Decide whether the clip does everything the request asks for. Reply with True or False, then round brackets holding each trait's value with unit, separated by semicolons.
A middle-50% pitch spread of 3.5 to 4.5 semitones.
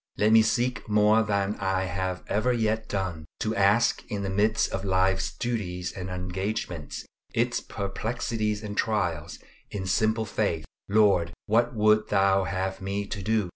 False (2.5 semitones)